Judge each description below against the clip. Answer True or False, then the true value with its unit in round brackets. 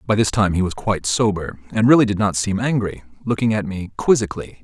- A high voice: False (105 Hz)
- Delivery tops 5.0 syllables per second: True (6.1 syllables/s)